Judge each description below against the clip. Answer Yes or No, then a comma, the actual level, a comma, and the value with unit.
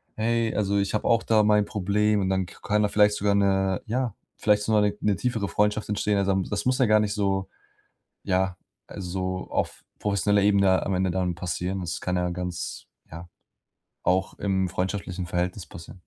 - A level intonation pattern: Yes, narrow, 2.2 semitones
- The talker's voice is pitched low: Yes, low, 100 Hz